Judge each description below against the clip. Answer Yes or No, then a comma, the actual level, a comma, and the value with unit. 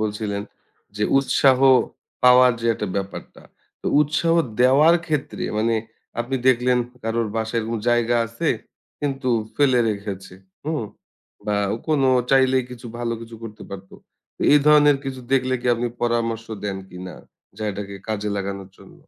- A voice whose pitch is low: Yes, low, 120 Hz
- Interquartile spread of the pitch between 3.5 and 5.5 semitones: Yes, average, 3.8 semitones